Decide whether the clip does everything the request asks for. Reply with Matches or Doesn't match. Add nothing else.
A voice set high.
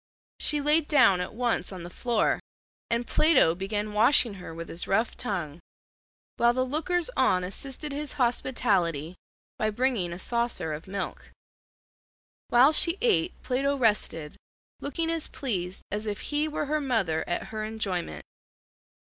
Matches